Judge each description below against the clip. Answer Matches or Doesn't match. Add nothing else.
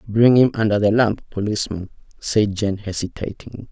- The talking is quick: Doesn't match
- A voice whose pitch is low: Matches